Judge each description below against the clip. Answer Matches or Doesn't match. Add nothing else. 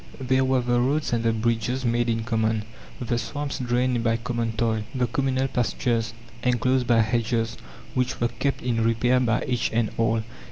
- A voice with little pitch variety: Matches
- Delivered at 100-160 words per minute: Doesn't match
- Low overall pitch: Matches